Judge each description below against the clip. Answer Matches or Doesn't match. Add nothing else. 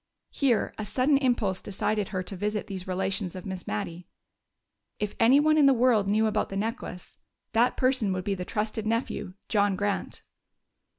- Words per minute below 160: Doesn't match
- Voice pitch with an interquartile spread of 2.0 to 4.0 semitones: Matches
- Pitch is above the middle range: Matches